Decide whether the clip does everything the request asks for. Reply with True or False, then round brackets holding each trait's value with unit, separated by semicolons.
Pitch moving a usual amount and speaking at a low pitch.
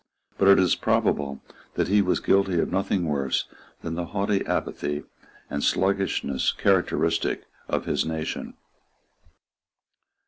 True (4.4 semitones; 90 Hz)